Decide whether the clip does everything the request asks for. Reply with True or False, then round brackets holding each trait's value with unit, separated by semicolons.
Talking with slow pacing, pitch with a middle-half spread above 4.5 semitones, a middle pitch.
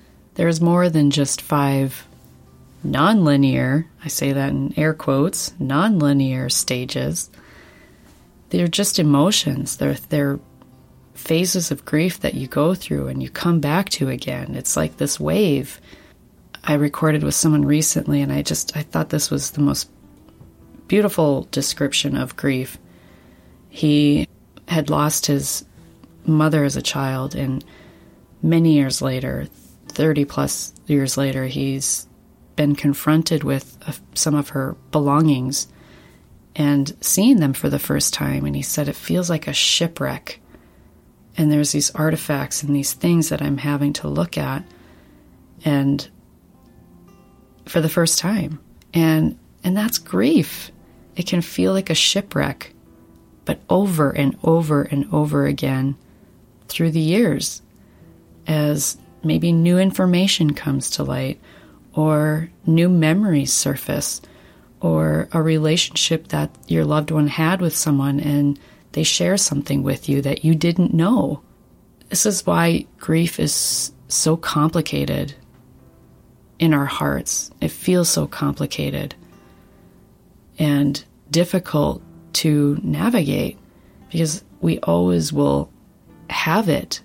False (130 wpm; 3.3 semitones; 145 Hz)